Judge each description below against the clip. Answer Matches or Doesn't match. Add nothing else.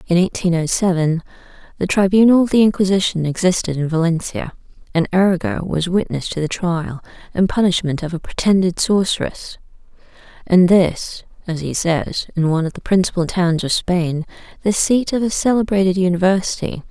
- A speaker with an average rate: Matches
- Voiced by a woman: Matches